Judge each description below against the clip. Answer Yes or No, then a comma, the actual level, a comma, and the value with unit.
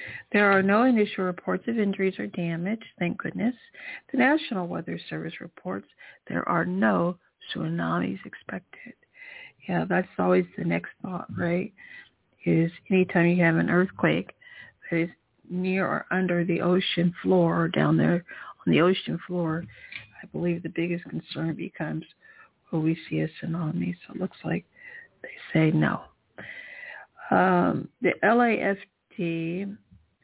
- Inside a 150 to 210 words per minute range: No, average, 140 wpm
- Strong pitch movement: No, average, 3.2 semitones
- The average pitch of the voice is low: No, medium, 180 Hz